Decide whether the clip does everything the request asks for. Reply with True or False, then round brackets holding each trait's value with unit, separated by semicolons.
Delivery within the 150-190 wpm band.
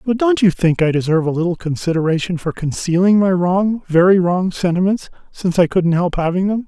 False (200 wpm)